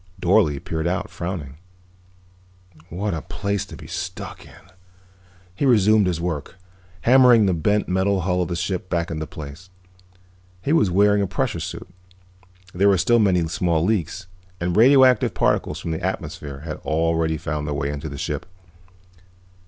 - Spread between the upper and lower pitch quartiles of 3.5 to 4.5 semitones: Yes, average, 4.0 semitones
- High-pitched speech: No, very low, 90 Hz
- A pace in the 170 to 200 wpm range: No, average, 160 wpm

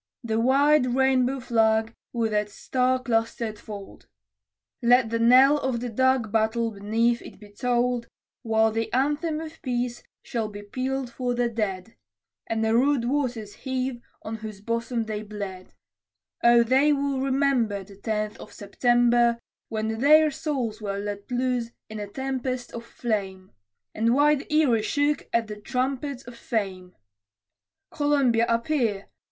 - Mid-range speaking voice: No, high, 235 Hz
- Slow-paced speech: No, average, 145 wpm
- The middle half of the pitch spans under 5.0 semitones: Yes, average, 3.1 semitones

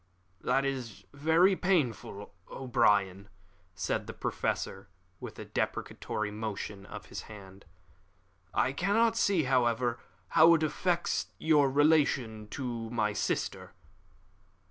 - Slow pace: Yes, slow, 110 wpm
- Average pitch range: No, wide, 6.8 semitones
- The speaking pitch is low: Yes, low, 125 Hz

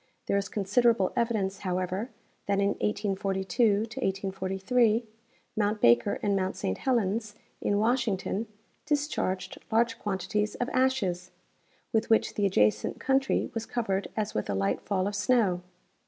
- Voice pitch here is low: No, high, 205 Hz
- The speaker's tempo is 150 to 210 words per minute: No, average, 140 wpm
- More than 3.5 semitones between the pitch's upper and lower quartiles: No, average, 3.2 semitones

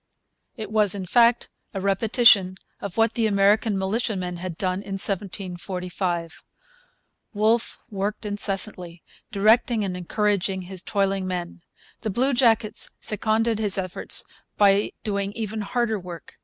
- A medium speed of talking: No, slow, 125 wpm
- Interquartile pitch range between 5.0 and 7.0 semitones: No, average, 2.7 semitones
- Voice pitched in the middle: No, high, 200 Hz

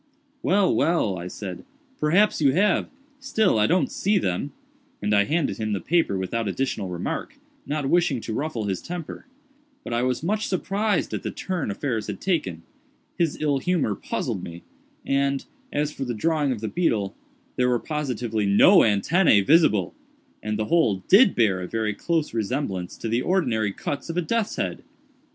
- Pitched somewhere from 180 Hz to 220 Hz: No, low, 135 Hz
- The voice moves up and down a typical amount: No, wide, 8.3 semitones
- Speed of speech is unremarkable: Yes, average, 170 wpm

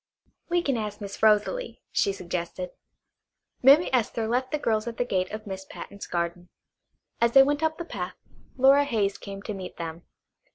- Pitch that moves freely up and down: Yes, wide, 5.8 semitones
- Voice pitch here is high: Yes, high, 215 Hz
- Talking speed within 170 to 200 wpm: Yes, average, 175 wpm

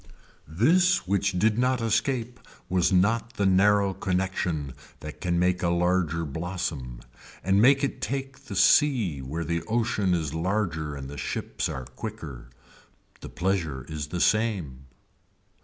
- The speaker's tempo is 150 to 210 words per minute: No, average, 140 wpm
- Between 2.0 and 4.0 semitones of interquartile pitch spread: No, wide, 5.4 semitones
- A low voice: Yes, very low, 90 Hz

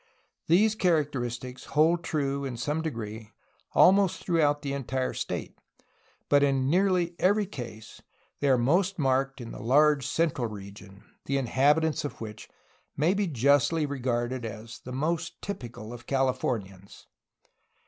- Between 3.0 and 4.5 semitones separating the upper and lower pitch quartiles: No, average, 5.1 semitones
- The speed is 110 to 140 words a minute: Yes, slow, 135 wpm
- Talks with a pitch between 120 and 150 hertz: Yes, low, 135 Hz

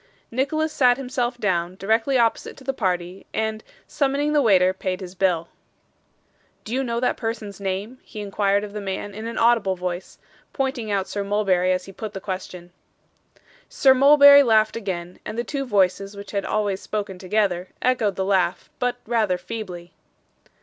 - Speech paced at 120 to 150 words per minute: No, average, 170 wpm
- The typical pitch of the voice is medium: No, high, 205 Hz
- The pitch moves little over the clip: No, average, 4.2 semitones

